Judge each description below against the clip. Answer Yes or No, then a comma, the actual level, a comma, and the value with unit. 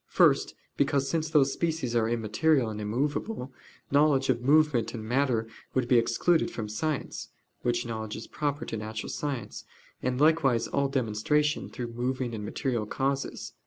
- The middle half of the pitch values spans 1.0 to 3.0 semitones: No, average, 4.2 semitones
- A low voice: Yes, low, 130 Hz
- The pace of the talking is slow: No, average, 155 wpm